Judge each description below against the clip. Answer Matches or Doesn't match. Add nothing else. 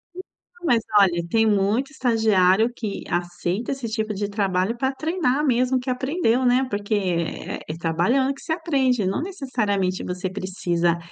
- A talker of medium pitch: Doesn't match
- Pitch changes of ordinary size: Doesn't match